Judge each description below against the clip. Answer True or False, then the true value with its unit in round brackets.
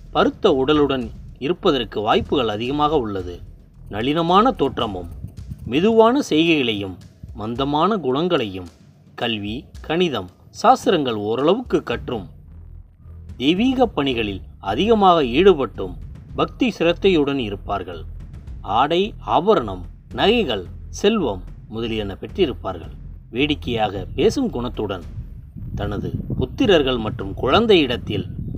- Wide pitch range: True (8.8 semitones)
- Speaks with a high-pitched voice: False (110 Hz)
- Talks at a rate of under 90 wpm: True (80 wpm)